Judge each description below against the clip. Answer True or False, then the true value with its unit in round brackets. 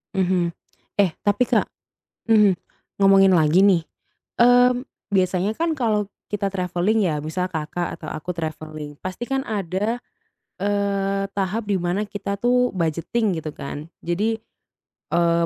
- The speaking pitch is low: False (195 Hz)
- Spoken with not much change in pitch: False (3.5 semitones)